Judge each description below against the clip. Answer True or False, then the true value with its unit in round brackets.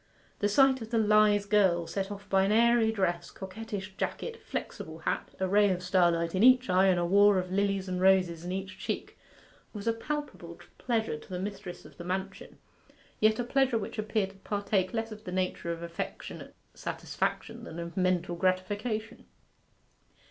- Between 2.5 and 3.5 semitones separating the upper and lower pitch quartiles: True (2.9 semitones)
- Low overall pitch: False (195 Hz)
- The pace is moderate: True (180 wpm)